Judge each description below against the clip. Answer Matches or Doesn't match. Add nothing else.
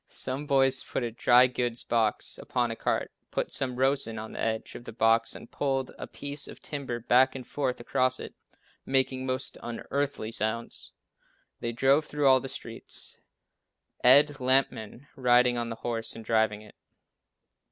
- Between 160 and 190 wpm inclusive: Matches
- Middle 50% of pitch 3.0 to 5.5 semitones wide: Doesn't match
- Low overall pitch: Matches